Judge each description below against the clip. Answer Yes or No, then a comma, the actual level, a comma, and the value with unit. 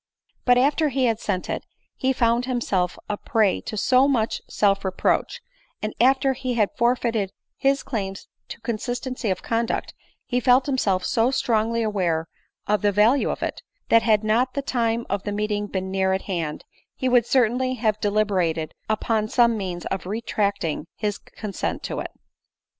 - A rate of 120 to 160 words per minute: No, average, 170 wpm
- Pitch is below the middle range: No, high, 220 Hz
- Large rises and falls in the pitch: No, average, 3.7 semitones